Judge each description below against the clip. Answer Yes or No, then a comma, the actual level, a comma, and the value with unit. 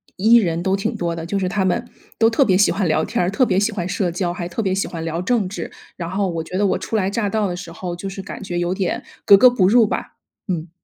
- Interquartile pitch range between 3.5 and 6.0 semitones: No, average, 2.7 semitones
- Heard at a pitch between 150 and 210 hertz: Yes, high, 190 Hz